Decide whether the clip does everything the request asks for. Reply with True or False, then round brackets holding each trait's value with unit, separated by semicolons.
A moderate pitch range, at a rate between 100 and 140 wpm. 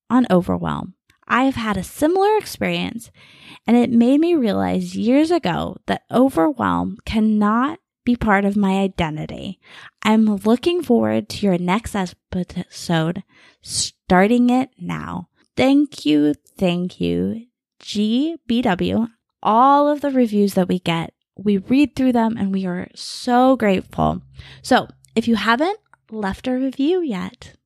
False (5.7 semitones; 135 wpm)